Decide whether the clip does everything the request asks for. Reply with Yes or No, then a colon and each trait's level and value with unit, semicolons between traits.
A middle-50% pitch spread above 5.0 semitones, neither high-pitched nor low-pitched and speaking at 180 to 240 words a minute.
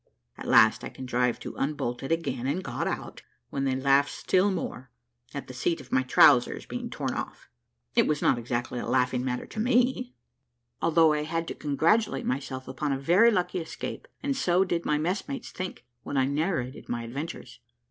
Yes: wide, 5.6 semitones; medium, 145 Hz; average, 190 wpm